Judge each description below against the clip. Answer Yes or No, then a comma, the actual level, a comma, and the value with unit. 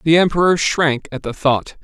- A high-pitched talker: No, medium, 150 Hz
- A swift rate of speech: No, average, 195 wpm